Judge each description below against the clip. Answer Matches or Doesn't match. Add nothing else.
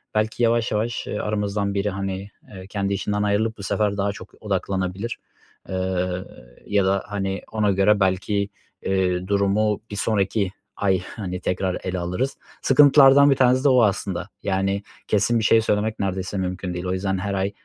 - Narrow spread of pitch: Matches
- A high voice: Doesn't match